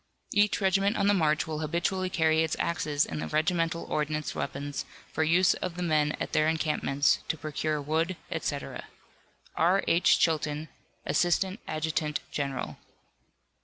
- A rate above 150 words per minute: No, average, 145 wpm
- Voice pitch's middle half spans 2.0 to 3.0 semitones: Yes, narrow, 2.6 semitones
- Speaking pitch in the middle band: Yes, medium, 160 Hz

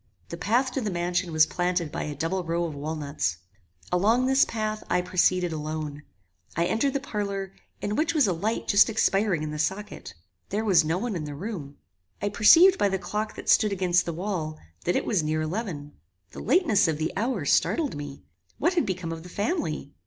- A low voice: No, medium, 185 Hz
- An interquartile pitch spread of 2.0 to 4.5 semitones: No, average, 5.2 semitones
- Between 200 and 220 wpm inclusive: Yes, fast, 205 wpm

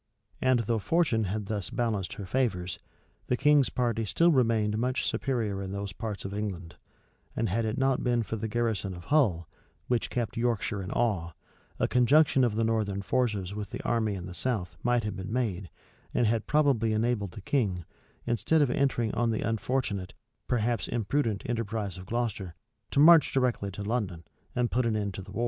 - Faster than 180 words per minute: Yes, average, 190 wpm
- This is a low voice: Yes, low, 110 Hz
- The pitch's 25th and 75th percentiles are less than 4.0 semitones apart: Yes, average, 3.6 semitones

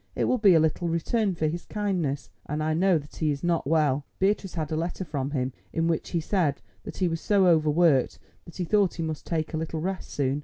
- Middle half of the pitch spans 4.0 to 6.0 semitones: No, average, 2.9 semitones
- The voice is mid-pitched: Yes, medium, 165 Hz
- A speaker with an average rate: No, fast, 240 wpm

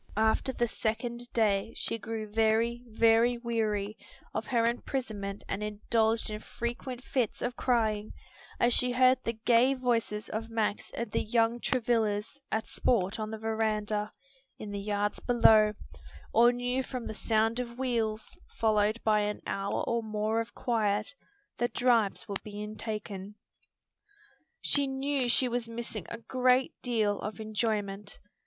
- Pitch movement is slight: Yes, narrow, 2.1 semitones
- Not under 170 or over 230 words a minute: No, average, 150 wpm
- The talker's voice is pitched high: Yes, high, 225 Hz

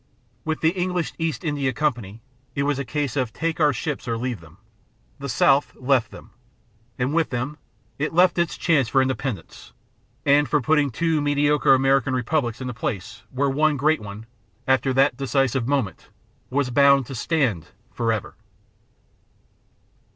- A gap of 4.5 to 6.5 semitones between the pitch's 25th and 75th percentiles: No, average, 3.2 semitones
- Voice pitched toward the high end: No, low, 135 Hz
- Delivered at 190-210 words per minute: No, average, 160 wpm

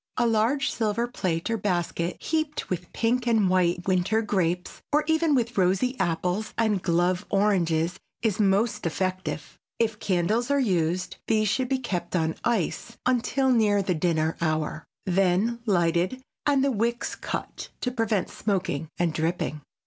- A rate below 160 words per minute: Yes, average, 150 wpm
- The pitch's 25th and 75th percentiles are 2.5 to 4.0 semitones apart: No, average, 4.9 semitones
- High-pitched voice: Yes, high, 195 Hz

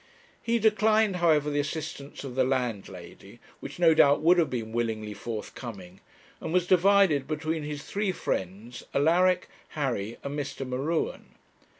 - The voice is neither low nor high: Yes, medium, 145 Hz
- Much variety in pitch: Yes, wide, 6.4 semitones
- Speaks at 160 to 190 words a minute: No, average, 140 wpm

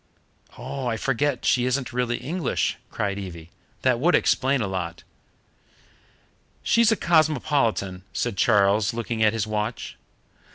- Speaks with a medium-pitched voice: No, low, 120 Hz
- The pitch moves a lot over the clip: No, average, 4.9 semitones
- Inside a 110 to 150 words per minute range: Yes, slow, 135 wpm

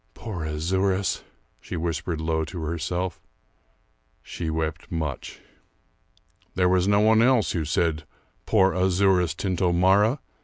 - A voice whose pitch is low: Yes, very low, 90 Hz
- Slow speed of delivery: Yes, slow, 115 wpm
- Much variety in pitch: No, average, 3.0 semitones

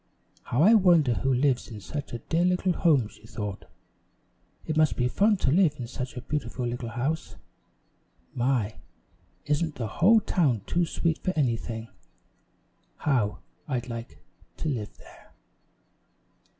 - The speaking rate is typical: Yes, average, 145 wpm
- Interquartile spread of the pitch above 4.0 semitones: Yes, wide, 5.4 semitones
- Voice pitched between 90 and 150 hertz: Yes, low, 135 Hz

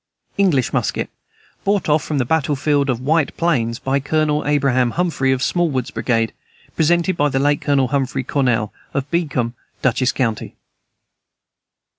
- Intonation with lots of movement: No, average, 3.2 semitones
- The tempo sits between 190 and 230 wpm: No, average, 145 wpm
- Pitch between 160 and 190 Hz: No, medium, 140 Hz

